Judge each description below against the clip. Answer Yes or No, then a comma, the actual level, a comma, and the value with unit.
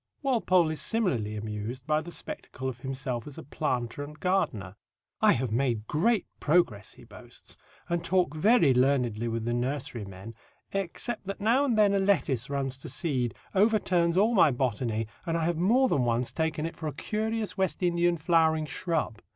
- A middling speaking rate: Yes, average, 180 wpm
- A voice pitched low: No, medium, 155 Hz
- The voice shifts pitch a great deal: Yes, wide, 7.0 semitones